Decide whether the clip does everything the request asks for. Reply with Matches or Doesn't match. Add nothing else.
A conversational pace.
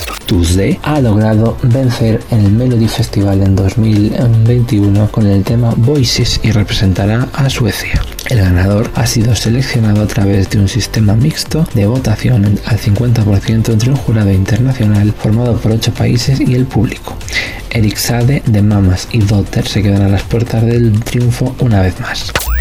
Matches